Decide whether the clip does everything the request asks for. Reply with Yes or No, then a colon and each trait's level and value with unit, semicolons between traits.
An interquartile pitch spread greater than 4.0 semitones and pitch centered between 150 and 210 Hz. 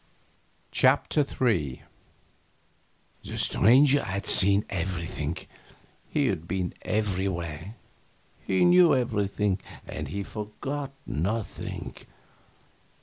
No: average, 5.2 semitones; low, 100 Hz